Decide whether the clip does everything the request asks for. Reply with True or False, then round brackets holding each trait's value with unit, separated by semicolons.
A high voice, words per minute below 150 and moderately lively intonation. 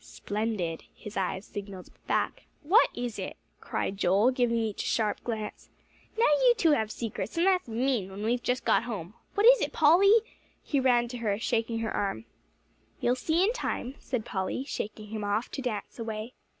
False (230 Hz; 185 wpm; 4.0 semitones)